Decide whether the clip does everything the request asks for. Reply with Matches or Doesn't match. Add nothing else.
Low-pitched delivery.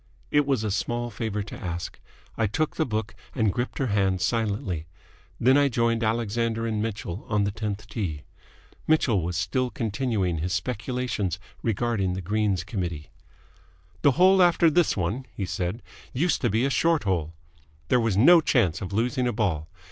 Matches